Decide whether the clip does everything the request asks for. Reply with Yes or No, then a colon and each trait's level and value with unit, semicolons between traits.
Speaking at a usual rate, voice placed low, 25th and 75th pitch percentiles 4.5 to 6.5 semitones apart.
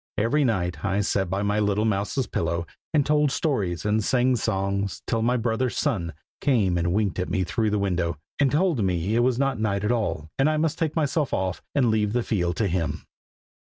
No: fast, 210 wpm; low, 105 Hz; average, 5.1 semitones